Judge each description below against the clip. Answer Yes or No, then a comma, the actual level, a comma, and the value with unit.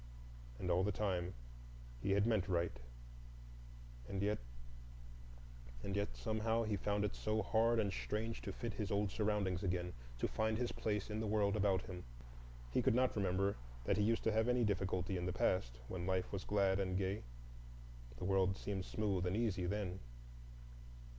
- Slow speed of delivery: No, average, 175 wpm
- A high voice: No, low, 100 Hz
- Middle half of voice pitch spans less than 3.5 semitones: Yes, average, 2.8 semitones